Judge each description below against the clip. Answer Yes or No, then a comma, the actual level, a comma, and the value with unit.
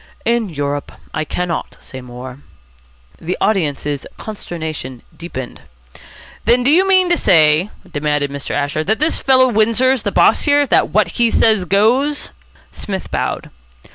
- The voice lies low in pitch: No, medium, 185 Hz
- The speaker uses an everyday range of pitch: No, wide, 8.4 semitones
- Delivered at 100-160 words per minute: Yes, average, 140 wpm